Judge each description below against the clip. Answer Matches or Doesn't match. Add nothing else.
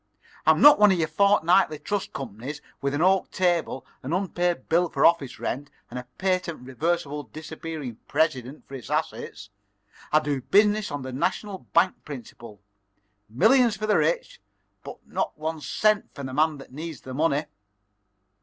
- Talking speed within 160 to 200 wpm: Matches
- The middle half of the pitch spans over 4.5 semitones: Matches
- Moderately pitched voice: Matches